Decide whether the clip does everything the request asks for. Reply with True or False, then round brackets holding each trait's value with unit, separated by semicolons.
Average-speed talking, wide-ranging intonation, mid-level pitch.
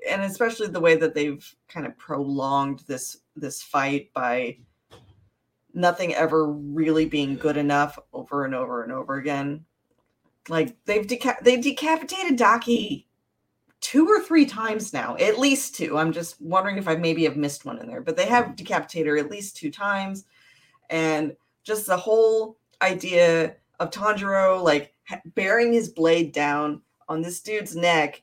True (160 wpm; 6.6 semitones; 165 Hz)